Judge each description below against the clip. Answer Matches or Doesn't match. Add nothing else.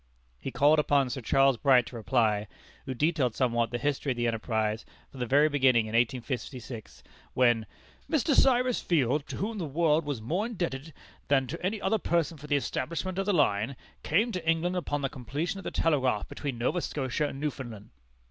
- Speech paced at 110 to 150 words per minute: Doesn't match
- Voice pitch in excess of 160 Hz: Doesn't match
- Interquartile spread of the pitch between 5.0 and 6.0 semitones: Matches